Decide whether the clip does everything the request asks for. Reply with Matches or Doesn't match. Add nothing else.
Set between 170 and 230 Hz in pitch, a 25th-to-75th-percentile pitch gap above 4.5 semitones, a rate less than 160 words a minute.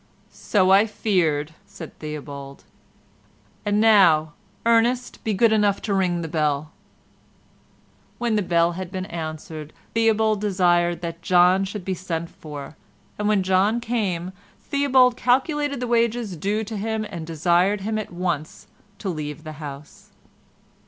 Matches